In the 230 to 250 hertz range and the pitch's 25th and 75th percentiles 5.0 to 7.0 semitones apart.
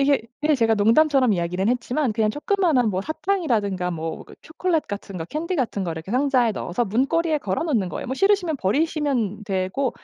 No: high, 245 Hz; wide, 7.4 semitones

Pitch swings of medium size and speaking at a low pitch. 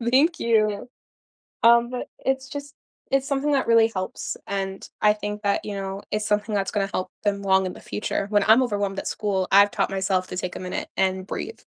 No: average, 3.2 semitones; high, 205 Hz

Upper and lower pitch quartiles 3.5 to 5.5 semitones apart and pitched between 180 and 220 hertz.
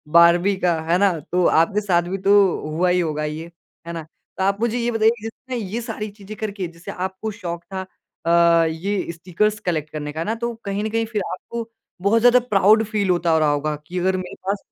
Yes: average, 4.0 semitones; high, 190 Hz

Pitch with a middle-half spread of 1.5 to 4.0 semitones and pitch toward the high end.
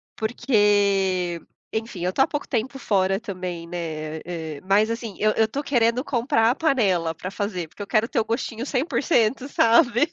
No: average, 4.7 semitones; high, 215 Hz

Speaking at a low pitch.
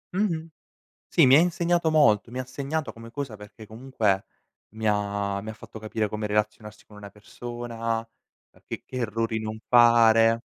Yes: low, 115 Hz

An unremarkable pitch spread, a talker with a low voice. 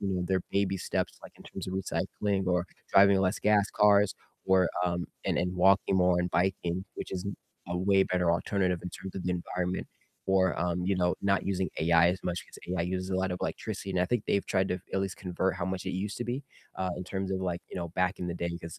No: narrow, 1.4 semitones; very low, 95 Hz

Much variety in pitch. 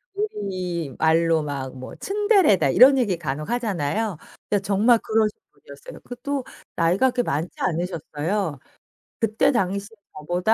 Yes: wide, 6.5 semitones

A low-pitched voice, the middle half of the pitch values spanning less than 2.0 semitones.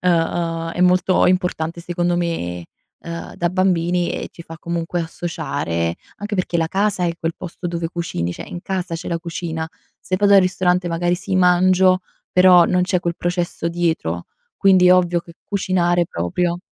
No: medium, 175 Hz; narrow, 1.5 semitones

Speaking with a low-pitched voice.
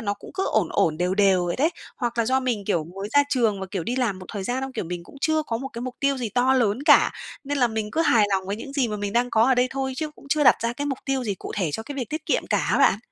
No: high, 235 Hz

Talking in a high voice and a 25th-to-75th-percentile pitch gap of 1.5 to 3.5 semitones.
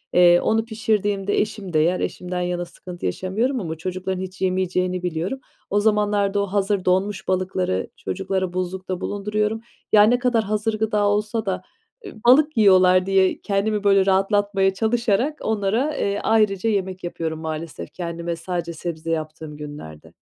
Yes: high, 195 Hz; average, 2.7 semitones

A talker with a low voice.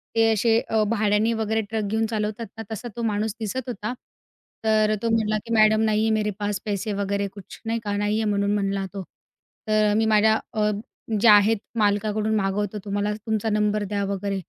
No: high, 210 Hz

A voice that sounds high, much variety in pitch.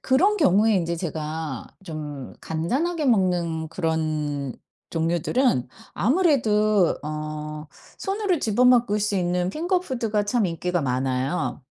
No: medium, 180 Hz; wide, 7.6 semitones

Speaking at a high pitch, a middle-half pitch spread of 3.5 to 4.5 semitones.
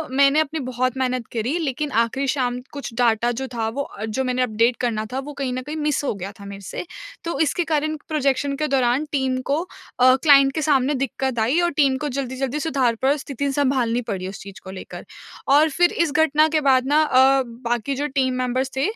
No: very high, 265 Hz; average, 2.9 semitones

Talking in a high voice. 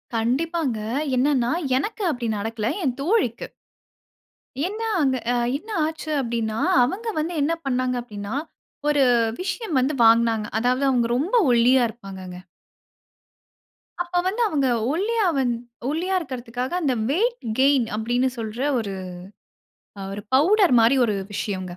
Yes: very high, 260 Hz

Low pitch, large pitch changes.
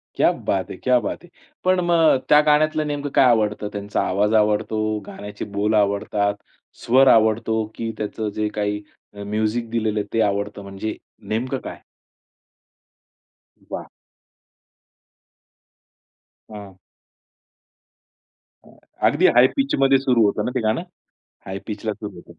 No: low, 110 Hz; average, 3.6 semitones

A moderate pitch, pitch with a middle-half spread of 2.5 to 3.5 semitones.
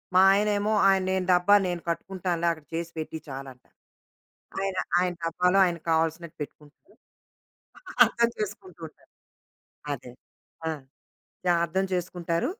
Yes: medium, 175 Hz; average, 2.8 semitones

